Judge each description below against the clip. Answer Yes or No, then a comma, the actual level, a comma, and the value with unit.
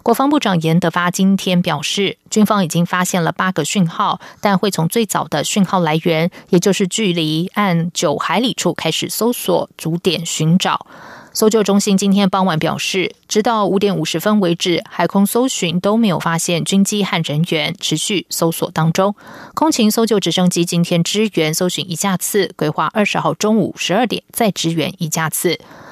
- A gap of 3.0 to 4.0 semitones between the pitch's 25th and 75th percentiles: Yes, average, 3.5 semitones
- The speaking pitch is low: No, medium, 180 Hz